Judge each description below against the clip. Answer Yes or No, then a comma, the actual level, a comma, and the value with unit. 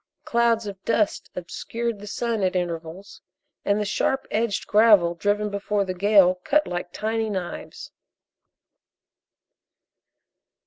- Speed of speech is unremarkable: No, slow, 120 wpm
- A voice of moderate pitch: No, high, 205 Hz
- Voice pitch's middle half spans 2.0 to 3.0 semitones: No, average, 3.4 semitones